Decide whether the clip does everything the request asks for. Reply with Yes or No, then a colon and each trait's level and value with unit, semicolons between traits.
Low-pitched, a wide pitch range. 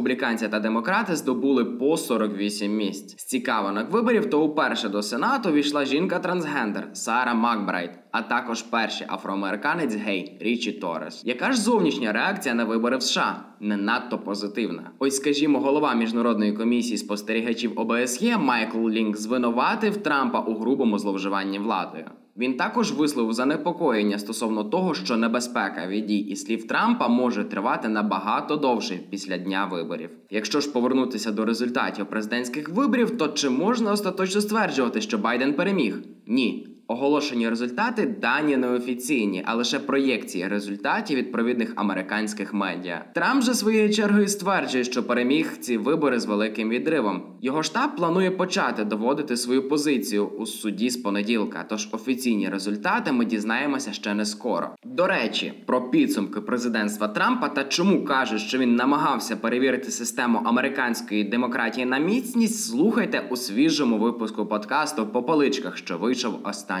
Yes: low, 120 Hz; wide, 6.1 semitones